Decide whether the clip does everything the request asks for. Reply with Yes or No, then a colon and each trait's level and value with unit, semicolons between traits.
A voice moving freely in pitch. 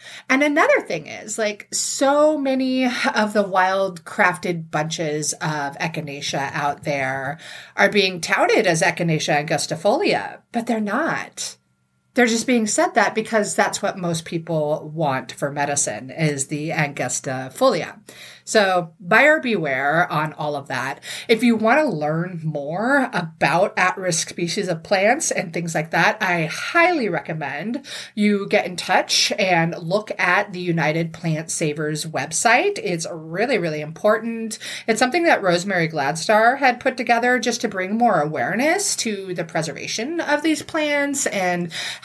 Yes: wide, 6.7 semitones